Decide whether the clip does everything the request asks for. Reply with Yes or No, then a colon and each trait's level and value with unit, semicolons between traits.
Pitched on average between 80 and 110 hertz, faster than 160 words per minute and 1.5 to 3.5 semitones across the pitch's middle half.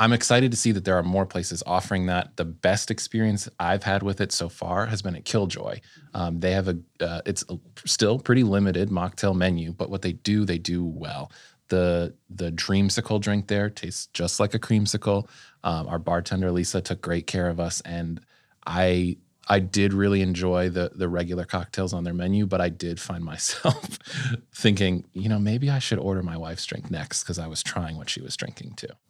Yes: very low, 95 Hz; fast, 205 wpm; average, 2.8 semitones